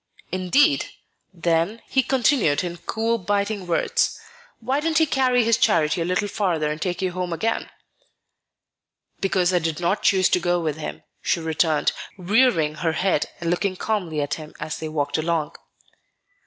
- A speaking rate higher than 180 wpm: No, average, 165 wpm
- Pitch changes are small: No, average, 4.6 semitones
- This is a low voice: No, medium, 180 Hz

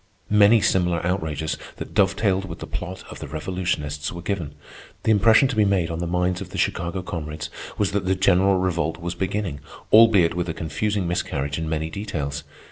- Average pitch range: Yes, average, 3.4 semitones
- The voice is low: Yes, very low, 90 Hz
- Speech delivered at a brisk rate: No, average, 190 wpm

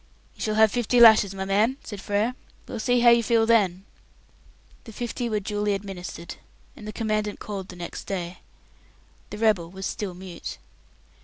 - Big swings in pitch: No, average, 2.8 semitones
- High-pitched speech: Yes, high, 210 Hz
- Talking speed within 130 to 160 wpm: No, average, 170 wpm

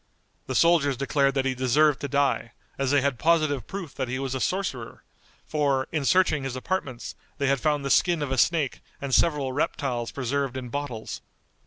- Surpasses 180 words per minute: Yes, average, 190 wpm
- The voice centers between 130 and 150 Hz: Yes, medium, 140 Hz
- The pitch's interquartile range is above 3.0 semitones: No, narrow, 2.5 semitones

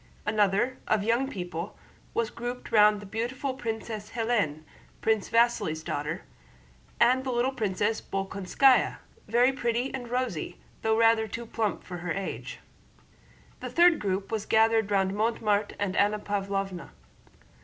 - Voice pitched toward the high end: Yes, high, 220 Hz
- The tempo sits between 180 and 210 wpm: No, slow, 135 wpm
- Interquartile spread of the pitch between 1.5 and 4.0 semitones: Yes, average, 3.2 semitones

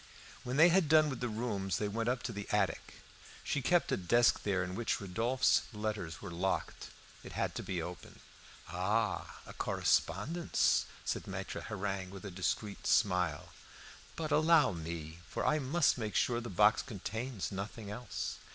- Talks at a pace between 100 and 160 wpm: No, average, 170 wpm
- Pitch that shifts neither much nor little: Yes, average, 4.7 semitones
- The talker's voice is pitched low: Yes, low, 105 Hz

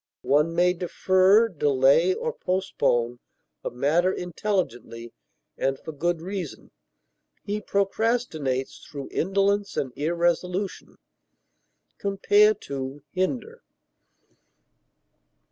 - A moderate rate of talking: No, slow, 80 wpm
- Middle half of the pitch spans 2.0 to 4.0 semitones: No, average, 5.3 semitones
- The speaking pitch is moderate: Yes, medium, 180 Hz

